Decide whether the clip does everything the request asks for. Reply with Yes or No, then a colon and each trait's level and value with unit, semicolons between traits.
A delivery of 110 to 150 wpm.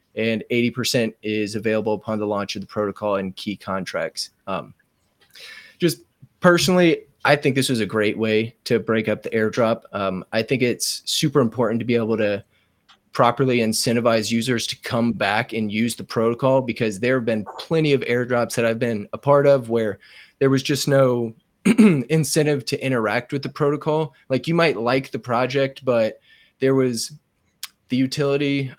No: average, 175 wpm